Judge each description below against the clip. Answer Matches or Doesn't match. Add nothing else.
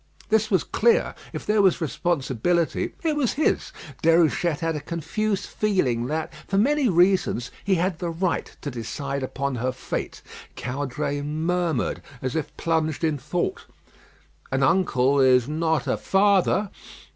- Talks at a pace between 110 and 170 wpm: Matches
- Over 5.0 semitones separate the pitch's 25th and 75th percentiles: Matches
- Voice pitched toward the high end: Doesn't match